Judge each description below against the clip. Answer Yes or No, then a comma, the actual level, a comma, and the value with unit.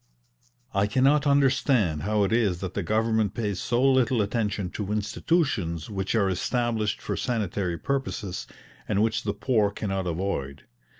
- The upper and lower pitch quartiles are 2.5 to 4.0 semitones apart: Yes, average, 3.6 semitones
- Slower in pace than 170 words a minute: Yes, average, 145 wpm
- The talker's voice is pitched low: Yes, low, 105 Hz